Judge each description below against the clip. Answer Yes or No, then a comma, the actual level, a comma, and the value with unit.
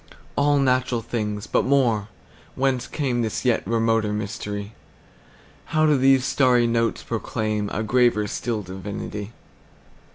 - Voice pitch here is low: Yes, low, 115 Hz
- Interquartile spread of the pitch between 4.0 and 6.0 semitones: No, average, 3.3 semitones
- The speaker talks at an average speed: No, slow, 100 wpm